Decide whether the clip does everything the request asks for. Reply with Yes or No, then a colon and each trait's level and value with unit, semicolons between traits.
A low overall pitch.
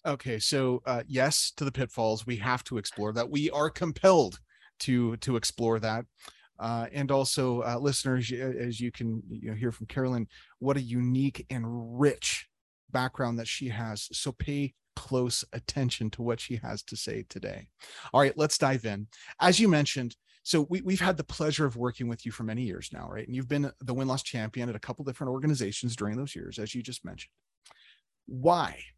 Yes: low, 125 Hz